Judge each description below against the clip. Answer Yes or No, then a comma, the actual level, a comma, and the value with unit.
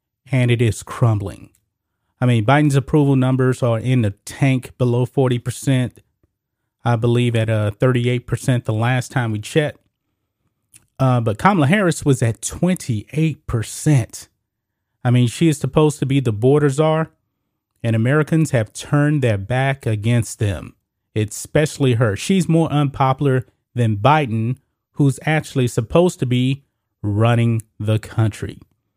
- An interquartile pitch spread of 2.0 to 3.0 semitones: No, average, 3.8 semitones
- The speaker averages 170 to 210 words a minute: No, average, 140 wpm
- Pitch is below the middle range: Yes, low, 125 Hz